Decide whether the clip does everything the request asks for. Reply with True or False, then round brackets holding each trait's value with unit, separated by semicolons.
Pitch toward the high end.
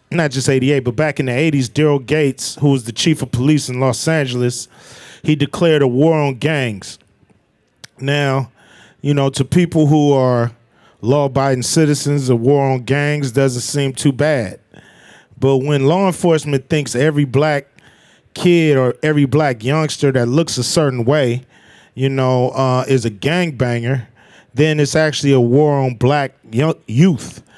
False (140 Hz)